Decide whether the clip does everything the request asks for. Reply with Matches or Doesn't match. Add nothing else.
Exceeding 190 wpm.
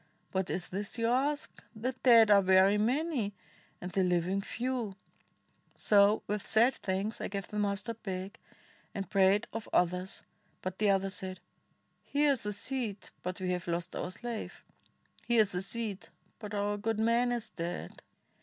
Doesn't match